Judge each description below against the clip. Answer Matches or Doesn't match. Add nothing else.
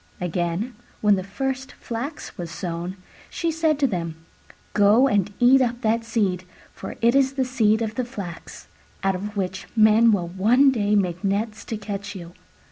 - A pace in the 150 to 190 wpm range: Matches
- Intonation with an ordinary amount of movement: Matches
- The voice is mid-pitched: Doesn't match